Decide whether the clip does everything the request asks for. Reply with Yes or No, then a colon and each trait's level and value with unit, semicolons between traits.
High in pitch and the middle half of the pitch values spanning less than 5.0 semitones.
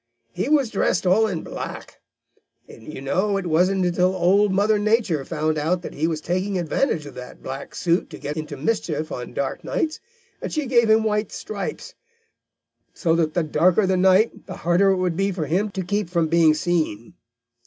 No: medium, 180 Hz; average, 4.3 semitones